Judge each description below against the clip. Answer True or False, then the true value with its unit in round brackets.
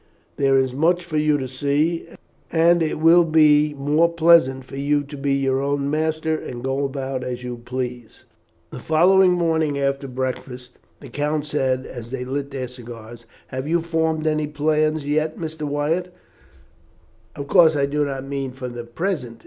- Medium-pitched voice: True (145 Hz)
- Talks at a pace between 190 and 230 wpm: False (175 wpm)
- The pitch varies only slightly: False (3.1 semitones)